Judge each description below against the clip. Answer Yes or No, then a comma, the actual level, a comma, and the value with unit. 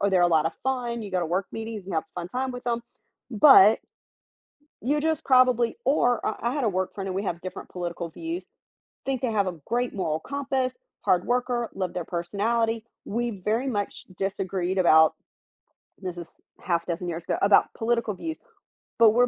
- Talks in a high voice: Yes, high, 210 Hz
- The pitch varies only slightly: No, average, 5.2 semitones